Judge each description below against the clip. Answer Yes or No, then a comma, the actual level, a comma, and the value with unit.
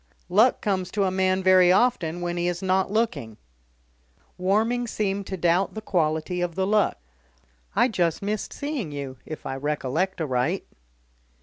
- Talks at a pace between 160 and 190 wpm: No, average, 150 wpm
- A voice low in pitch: No, medium, 185 Hz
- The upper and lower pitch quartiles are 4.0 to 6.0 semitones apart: No, average, 3.4 semitones